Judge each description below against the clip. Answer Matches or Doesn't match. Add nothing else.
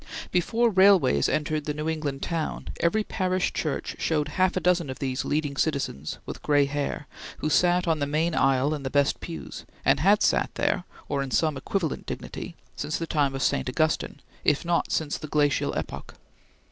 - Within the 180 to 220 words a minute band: Matches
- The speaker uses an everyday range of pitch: Matches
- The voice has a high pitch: Doesn't match